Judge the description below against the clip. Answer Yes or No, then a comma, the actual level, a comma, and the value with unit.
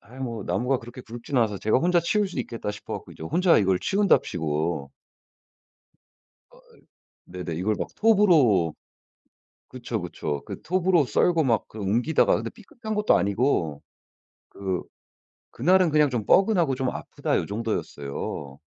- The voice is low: Yes, low, 120 Hz